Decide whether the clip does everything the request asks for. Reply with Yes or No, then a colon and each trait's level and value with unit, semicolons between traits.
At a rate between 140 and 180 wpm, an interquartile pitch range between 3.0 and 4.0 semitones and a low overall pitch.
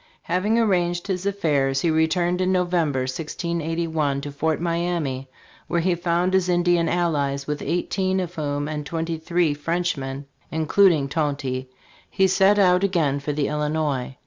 No: average, 150 wpm; average, 3.5 semitones; medium, 165 Hz